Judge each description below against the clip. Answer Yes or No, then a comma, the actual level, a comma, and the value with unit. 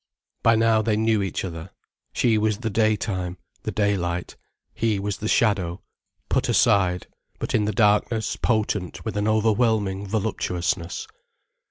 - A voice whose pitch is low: Yes, low, 105 Hz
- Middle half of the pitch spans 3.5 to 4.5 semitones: No, average, 2.7 semitones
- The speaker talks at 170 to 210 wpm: No, average, 140 wpm